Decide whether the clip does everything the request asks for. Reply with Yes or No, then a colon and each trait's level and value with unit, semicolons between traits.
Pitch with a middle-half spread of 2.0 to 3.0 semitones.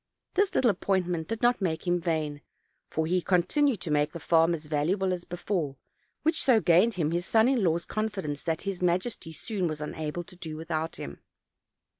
No: average, 3.8 semitones